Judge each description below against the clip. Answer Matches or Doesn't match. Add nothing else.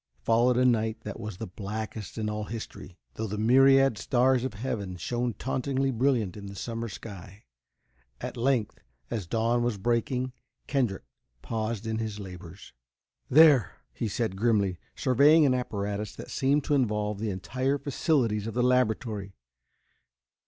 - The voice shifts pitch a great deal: Doesn't match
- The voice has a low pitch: Matches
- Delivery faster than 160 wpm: Doesn't match